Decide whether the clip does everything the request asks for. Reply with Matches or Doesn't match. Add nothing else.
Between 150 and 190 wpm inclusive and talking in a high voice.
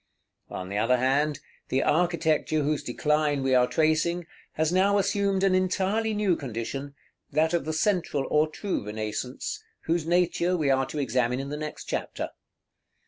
Doesn't match